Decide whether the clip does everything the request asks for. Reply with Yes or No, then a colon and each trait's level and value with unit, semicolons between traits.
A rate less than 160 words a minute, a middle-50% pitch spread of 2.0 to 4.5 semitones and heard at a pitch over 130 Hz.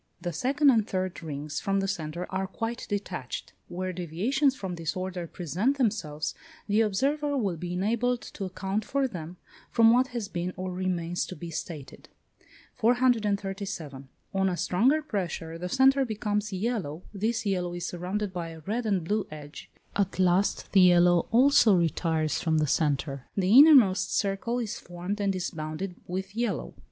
No: average, 165 wpm; average, 4.2 semitones; high, 190 Hz